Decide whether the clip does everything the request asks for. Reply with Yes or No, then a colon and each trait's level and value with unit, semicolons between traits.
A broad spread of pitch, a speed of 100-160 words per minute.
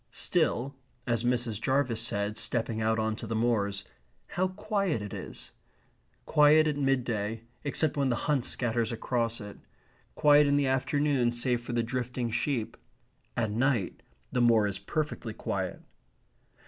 No: average, 4.0 semitones; average, 150 wpm